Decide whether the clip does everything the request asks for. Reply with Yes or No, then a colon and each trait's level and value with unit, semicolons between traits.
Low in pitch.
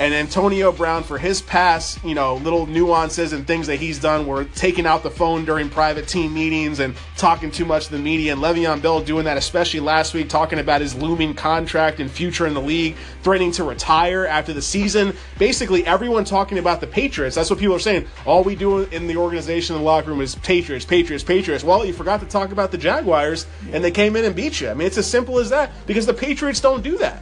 No: medium, 165 Hz